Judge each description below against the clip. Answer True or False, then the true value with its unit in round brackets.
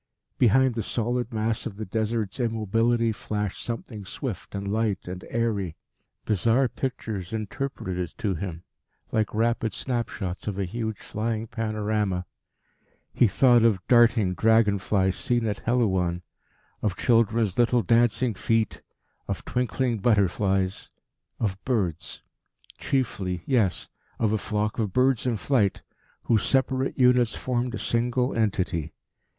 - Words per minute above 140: False (135 wpm)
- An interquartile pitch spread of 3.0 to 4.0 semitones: True (3.3 semitones)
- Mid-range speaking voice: False (110 Hz)